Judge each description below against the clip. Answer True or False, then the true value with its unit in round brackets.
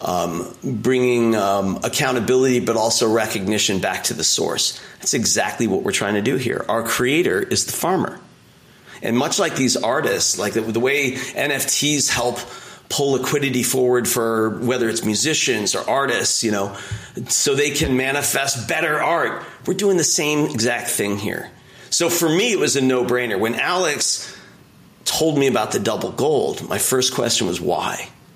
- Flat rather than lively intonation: False (3.7 semitones)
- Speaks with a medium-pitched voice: False (125 Hz)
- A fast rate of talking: False (170 wpm)